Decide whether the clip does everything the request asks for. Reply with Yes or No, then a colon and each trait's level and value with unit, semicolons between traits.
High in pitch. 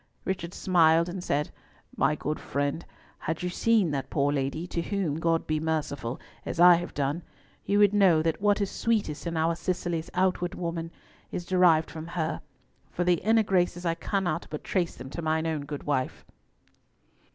No: medium, 170 Hz